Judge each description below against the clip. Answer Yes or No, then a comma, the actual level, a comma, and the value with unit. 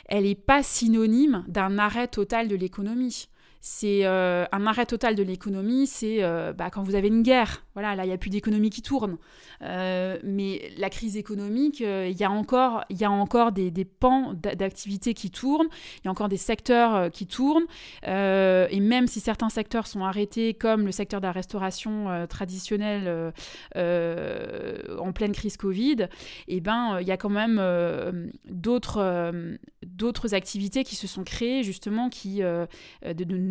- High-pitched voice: Yes, high, 205 Hz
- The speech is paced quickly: No, average, 180 wpm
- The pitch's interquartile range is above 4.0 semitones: No, average, 3.3 semitones